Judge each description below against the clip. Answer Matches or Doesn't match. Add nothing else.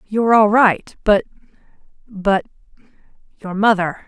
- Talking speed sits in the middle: Doesn't match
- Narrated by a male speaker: Doesn't match